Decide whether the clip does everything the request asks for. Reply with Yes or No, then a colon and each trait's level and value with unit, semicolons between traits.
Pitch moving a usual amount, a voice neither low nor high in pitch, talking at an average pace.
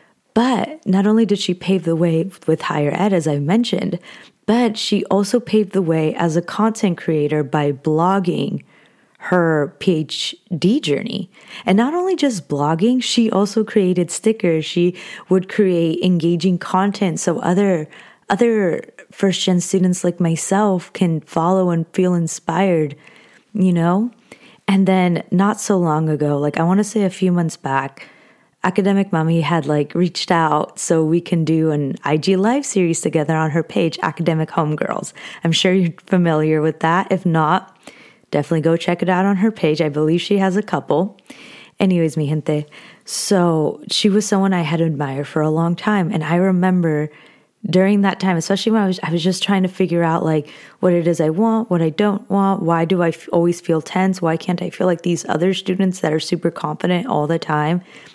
Yes: average, 3.4 semitones; medium, 180 Hz; average, 185 wpm